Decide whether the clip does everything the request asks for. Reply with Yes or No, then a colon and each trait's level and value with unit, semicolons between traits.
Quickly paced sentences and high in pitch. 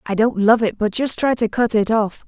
Yes: fast, 290 wpm; high, 220 Hz